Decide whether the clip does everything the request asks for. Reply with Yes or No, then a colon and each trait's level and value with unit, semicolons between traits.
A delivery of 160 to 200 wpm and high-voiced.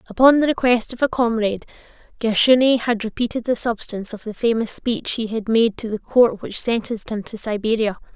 Yes: average, 190 wpm; high, 225 Hz